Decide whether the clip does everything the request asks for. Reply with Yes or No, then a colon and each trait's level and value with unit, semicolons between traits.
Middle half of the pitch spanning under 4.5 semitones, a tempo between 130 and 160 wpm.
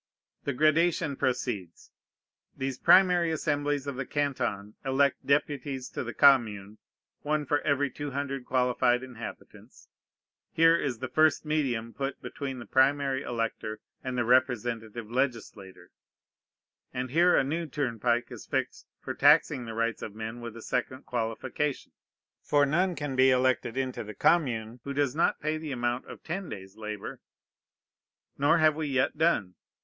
Yes: average, 3.6 semitones; average, 150 wpm